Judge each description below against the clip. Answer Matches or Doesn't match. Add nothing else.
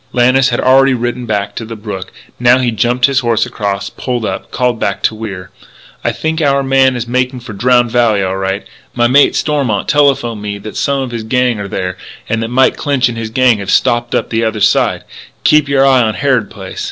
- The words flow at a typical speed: Doesn't match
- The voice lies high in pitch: Doesn't match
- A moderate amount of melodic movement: Matches